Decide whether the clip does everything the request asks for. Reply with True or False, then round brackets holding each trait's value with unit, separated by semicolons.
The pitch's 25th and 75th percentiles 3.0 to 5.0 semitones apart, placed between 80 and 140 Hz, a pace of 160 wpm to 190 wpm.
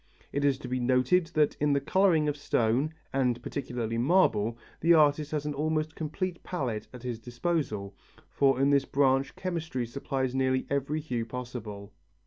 True (3.8 semitones; 135 Hz; 165 wpm)